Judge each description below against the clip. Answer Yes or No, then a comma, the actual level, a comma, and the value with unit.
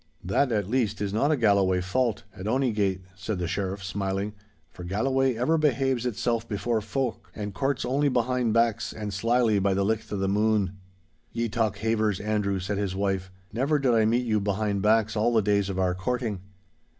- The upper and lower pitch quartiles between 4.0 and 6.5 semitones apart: No, average, 3.4 semitones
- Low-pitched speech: Yes, low, 105 Hz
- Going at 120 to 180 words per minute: No, average, 195 wpm